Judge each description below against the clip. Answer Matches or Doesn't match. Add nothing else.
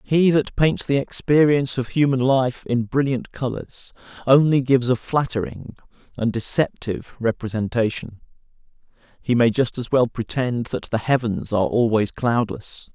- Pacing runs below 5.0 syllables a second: Matches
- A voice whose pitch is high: Doesn't match